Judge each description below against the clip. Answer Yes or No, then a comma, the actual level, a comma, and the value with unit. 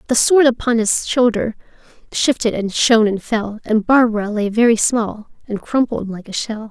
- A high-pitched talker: Yes, high, 225 Hz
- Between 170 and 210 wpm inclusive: Yes, average, 180 wpm